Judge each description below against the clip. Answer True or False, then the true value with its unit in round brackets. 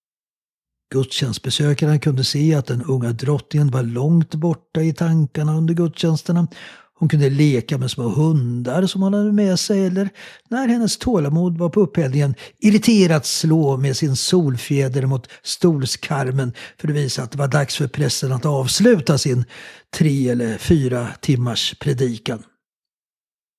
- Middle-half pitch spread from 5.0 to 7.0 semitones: False (4.3 semitones)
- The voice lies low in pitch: False (150 Hz)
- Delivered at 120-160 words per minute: True (140 wpm)